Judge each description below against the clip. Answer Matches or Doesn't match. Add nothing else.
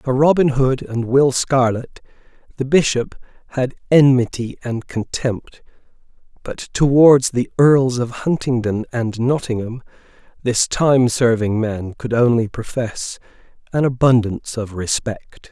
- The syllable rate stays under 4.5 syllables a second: Matches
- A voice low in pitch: Matches